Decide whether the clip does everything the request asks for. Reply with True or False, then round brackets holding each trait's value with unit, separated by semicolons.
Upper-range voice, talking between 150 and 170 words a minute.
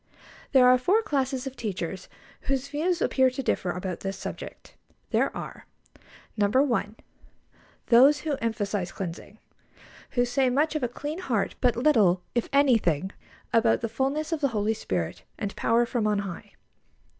True (240 Hz; 155 wpm)